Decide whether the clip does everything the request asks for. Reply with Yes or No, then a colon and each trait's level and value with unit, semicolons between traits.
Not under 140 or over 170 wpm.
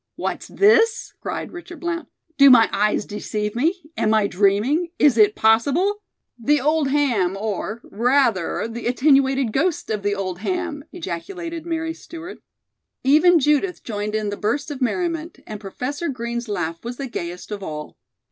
Yes: average, 160 wpm